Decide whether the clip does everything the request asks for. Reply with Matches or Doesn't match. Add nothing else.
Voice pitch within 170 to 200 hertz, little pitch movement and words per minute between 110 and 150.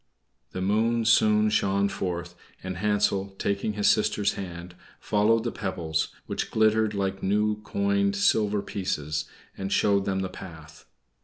Doesn't match